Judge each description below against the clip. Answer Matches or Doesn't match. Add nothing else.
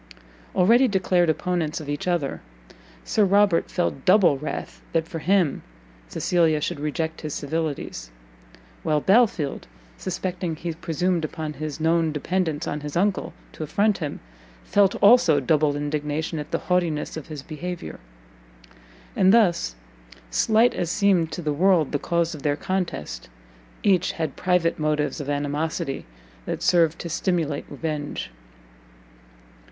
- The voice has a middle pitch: Matches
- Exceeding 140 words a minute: Doesn't match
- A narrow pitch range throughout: Doesn't match